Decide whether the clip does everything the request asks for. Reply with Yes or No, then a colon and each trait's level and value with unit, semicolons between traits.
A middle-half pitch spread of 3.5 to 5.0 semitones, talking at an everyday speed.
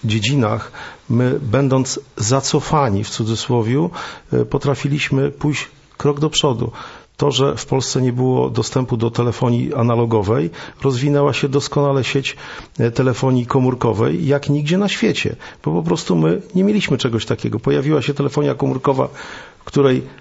No: average, 3.1 semitones; average, 130 wpm